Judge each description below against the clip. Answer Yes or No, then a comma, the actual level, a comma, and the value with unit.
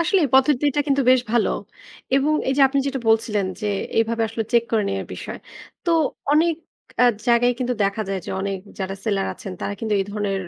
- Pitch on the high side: Yes, high, 230 Hz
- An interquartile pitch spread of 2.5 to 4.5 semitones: No, average, 5.0 semitones